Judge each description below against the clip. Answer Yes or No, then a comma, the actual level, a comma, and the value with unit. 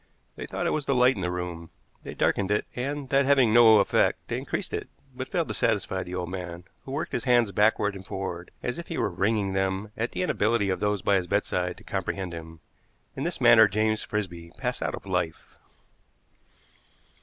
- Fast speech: Yes, fast, 210 wpm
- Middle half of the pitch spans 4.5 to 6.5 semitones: Yes, average, 4.9 semitones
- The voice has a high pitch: No, low, 105 Hz